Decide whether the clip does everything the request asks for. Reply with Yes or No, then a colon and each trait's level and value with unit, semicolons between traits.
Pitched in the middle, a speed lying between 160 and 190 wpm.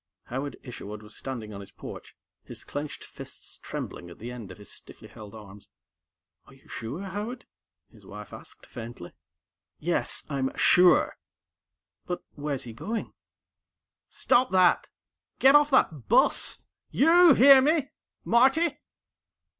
No: medium, 145 Hz; average, 140 wpm